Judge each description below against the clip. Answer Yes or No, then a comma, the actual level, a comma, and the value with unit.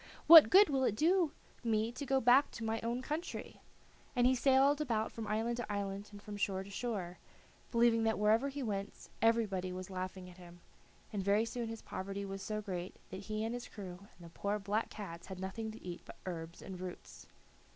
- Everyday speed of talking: No, fast, 210 wpm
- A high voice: Yes, high, 215 Hz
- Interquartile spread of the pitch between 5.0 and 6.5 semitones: No, average, 3.9 semitones